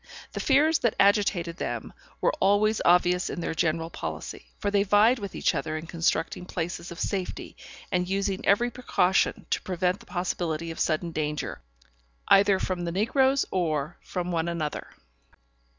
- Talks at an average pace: Yes, average, 160 wpm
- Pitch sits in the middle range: Yes, medium, 180 Hz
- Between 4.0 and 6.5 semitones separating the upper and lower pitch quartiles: No, average, 3.3 semitones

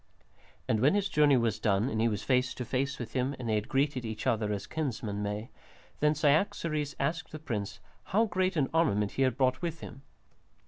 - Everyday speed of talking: No, fast, 210 wpm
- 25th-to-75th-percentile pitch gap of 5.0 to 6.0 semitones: Yes, wide, 5.4 semitones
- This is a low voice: Yes, low, 130 Hz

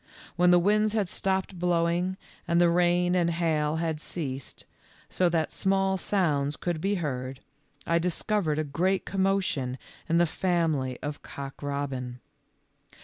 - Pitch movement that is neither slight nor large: Yes, average, 3.8 semitones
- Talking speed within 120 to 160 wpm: Yes, average, 145 wpm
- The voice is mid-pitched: Yes, medium, 170 Hz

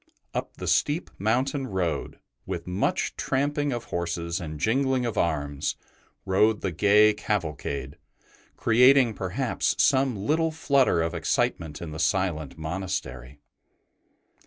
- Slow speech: Yes, slow, 120 wpm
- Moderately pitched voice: No, very low, 95 Hz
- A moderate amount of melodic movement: No, wide, 7.7 semitones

